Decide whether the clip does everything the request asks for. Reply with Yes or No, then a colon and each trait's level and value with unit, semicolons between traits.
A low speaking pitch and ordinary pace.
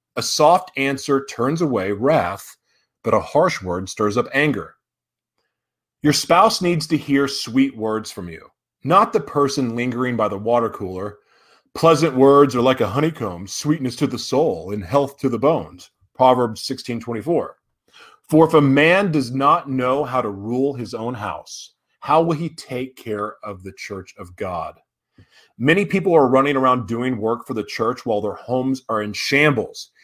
Yes: low, 130 Hz; average, 170 wpm